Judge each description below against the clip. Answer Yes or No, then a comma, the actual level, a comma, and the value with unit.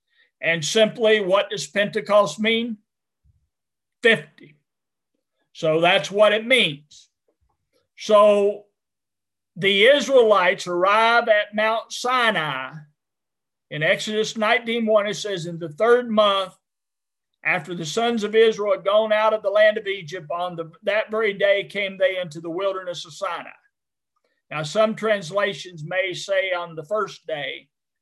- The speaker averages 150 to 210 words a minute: No, slow, 135 wpm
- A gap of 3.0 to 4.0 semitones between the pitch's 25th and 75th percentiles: Yes, average, 3.6 semitones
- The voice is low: No, high, 205 Hz